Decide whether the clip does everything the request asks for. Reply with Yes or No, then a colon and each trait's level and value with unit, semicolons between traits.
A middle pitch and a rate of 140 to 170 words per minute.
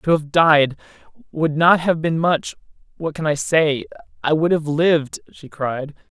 Yes: medium, 155 Hz; average, 155 wpm